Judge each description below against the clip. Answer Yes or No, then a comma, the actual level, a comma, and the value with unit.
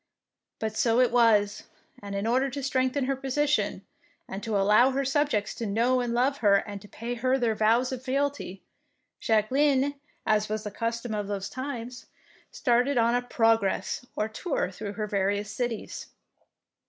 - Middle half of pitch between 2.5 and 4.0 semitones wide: Yes, average, 3.6 semitones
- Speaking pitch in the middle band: No, high, 235 Hz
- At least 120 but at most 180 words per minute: Yes, average, 165 wpm